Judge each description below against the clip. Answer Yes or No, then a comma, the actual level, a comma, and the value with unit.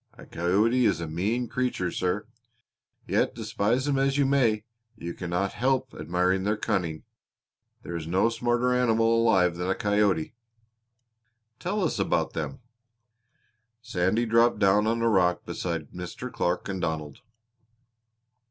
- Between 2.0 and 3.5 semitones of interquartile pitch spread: No, average, 5.2 semitones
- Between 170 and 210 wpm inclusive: No, average, 140 wpm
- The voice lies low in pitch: Yes, low, 105 Hz